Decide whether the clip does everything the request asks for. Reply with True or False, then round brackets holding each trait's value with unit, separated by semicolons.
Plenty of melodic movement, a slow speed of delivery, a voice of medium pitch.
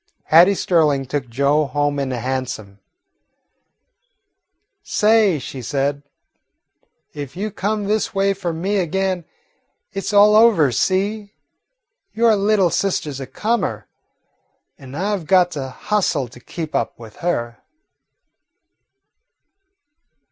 True (6.6 semitones; 120 wpm; 170 Hz)